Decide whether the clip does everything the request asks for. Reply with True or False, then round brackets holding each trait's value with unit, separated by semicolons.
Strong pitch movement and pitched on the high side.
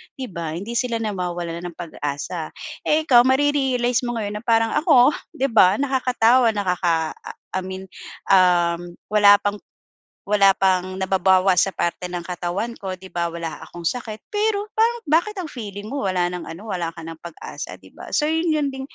True (6.1 semitones; 200 Hz)